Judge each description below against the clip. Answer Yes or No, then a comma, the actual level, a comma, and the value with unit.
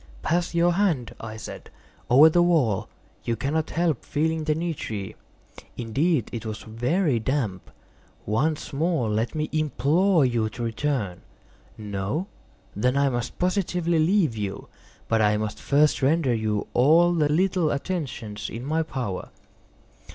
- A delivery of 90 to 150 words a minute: Yes, average, 140 wpm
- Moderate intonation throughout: No, wide, 6.4 semitones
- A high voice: No, medium, 140 Hz